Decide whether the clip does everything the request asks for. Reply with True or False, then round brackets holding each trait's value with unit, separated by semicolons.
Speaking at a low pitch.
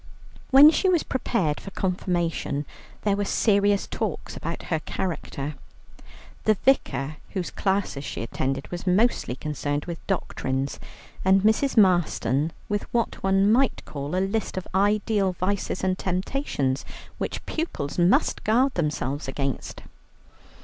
False (185 Hz)